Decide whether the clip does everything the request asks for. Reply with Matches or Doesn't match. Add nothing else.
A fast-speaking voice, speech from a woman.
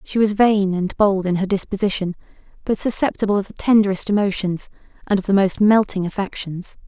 Doesn't match